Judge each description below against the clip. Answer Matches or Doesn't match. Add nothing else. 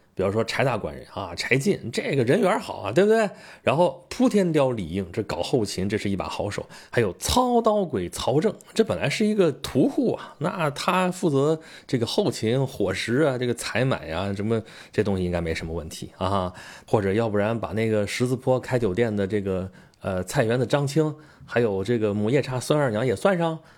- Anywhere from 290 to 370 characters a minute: Matches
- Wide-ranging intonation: Matches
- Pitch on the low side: Matches